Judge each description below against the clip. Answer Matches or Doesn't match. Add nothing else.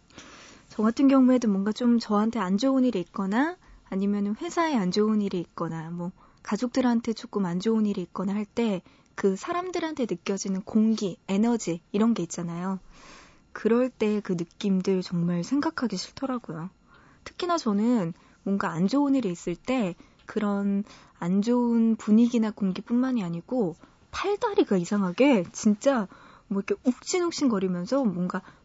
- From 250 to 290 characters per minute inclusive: Doesn't match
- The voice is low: Doesn't match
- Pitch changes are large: Doesn't match